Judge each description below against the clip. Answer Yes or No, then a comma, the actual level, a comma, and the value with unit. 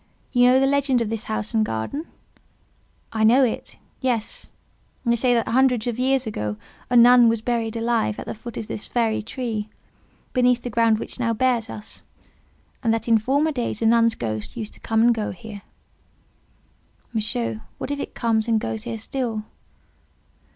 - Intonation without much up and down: Yes, narrow, 2.3 semitones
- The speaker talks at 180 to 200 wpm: Yes, average, 185 wpm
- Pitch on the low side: No, high, 230 Hz